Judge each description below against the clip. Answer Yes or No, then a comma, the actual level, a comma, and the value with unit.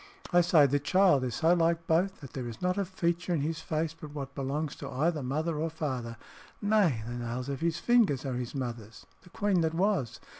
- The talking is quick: Yes, fast, 220 wpm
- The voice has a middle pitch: Yes, medium, 155 Hz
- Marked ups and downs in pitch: No, average, 4.6 semitones